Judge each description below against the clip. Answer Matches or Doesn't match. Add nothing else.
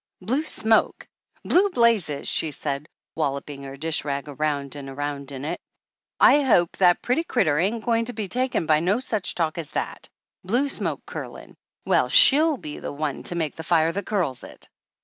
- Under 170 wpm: Doesn't match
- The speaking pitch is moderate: Matches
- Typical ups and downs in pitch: Doesn't match